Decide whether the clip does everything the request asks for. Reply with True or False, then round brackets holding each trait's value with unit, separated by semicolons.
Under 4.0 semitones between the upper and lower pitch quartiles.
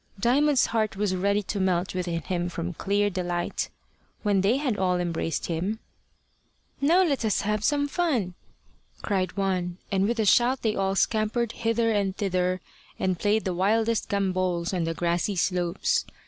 True (3.6 semitones)